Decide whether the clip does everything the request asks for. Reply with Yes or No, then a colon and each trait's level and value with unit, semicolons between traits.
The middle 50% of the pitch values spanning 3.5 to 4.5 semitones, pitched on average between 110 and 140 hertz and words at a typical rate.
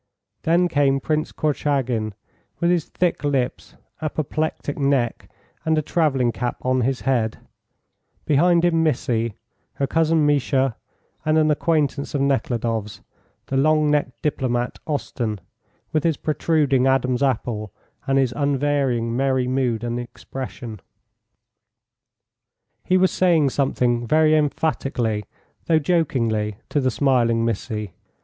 No: average, 4.2 semitones; low, 135 Hz; slow, 120 wpm